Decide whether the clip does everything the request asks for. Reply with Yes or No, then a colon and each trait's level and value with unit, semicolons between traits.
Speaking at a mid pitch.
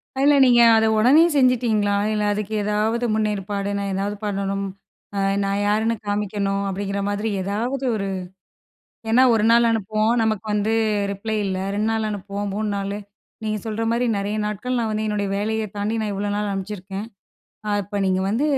No: high, 210 Hz